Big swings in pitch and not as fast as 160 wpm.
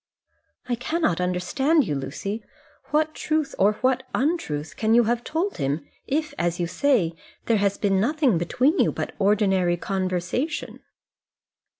Yes: wide, 8.1 semitones; average, 140 wpm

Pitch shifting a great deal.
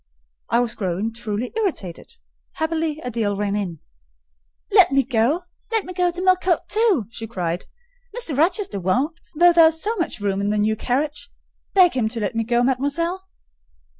Yes: wide, 8.1 semitones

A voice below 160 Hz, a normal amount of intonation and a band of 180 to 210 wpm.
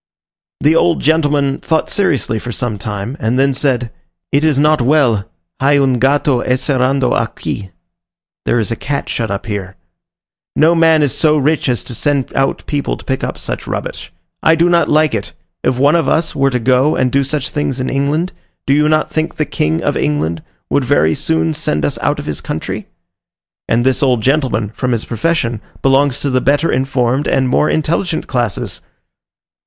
Yes: low, 135 Hz; average, 3.8 semitones; average, 190 wpm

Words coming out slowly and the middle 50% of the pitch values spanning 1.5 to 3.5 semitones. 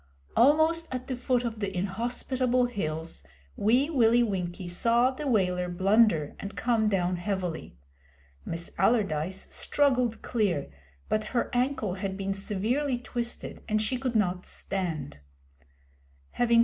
No: slow, 125 wpm; average, 5.0 semitones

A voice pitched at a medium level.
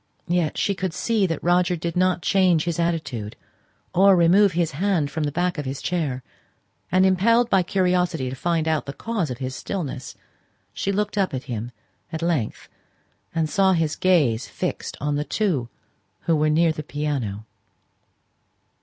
Yes: medium, 165 Hz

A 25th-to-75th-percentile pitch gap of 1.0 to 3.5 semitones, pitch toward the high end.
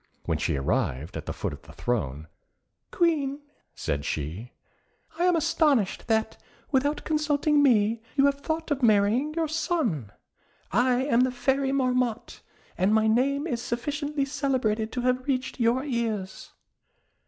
No: average, 4.7 semitones; very high, 255 Hz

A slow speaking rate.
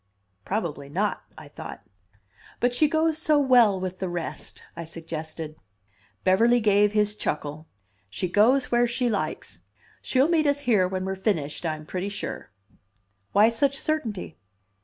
No: average, 145 wpm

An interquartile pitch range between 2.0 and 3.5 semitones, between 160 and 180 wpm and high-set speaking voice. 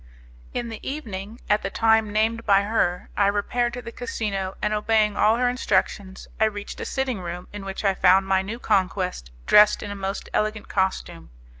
No: narrow, 2.6 semitones; average, 190 wpm; high, 205 Hz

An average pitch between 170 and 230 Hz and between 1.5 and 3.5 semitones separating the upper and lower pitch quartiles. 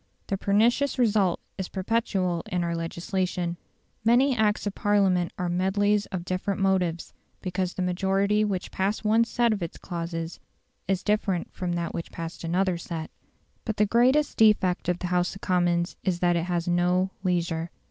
Yes: medium, 185 Hz; average, 2.8 semitones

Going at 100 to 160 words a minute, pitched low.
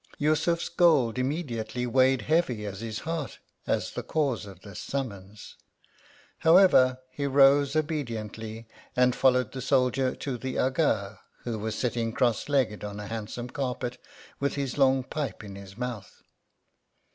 Yes: average, 145 wpm; low, 125 Hz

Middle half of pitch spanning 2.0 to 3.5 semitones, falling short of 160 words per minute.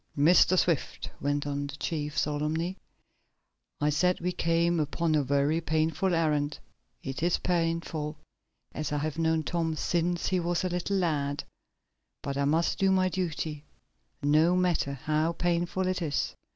Yes: average, 2.8 semitones; average, 150 wpm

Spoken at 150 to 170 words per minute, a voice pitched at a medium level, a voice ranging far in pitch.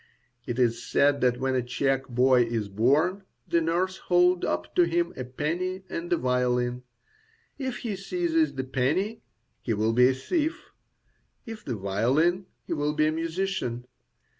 Yes: average, 165 wpm; medium, 145 Hz; wide, 6.5 semitones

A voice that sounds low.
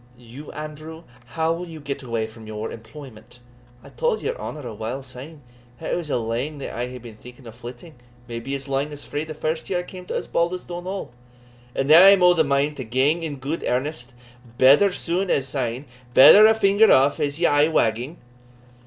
No: medium, 145 Hz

